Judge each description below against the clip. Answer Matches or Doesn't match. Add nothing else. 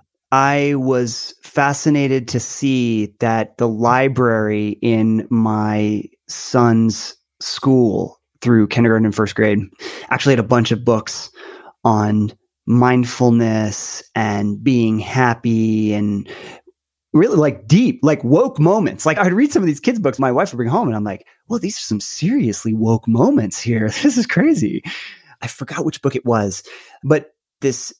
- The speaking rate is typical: Matches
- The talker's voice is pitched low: Matches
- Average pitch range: Matches